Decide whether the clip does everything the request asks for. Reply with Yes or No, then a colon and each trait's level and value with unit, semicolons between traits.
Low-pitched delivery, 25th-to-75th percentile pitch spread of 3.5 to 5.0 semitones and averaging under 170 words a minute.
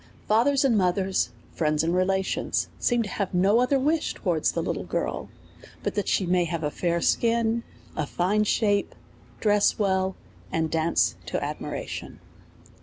No: high, 195 Hz; average, 4.2 semitones; average, 160 wpm